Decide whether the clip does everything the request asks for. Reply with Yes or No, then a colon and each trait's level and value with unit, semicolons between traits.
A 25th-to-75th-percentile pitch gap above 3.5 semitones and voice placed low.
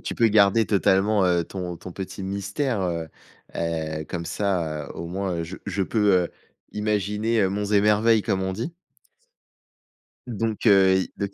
No: average, 2.7 semitones; low, 100 Hz